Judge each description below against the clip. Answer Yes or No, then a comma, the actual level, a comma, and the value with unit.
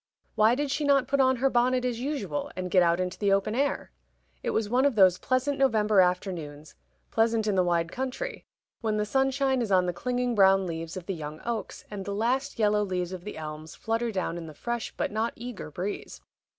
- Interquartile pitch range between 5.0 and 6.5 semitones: Yes, wide, 5.5 semitones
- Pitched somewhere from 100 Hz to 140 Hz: No, high, 210 Hz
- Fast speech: Yes, fast, 215 wpm